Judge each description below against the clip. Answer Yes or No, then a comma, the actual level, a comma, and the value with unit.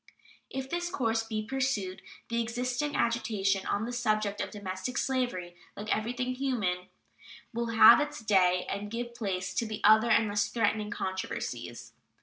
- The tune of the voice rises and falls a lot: No, average, 3.3 semitones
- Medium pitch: No, high, 220 Hz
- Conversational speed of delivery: Yes, average, 145 wpm